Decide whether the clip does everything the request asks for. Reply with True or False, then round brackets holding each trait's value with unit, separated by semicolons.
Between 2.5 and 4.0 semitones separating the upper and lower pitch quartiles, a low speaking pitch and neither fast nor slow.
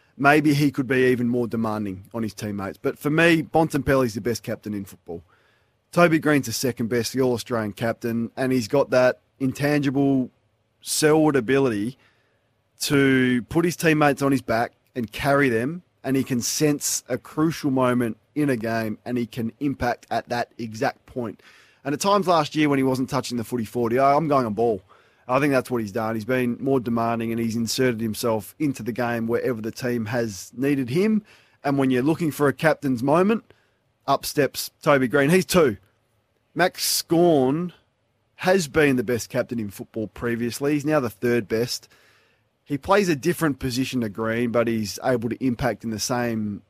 True (3.7 semitones; 125 Hz; 190 wpm)